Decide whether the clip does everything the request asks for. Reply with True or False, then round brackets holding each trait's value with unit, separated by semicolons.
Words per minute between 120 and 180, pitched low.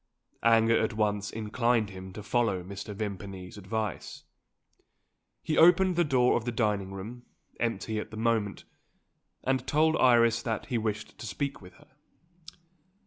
True (145 wpm; 110 Hz)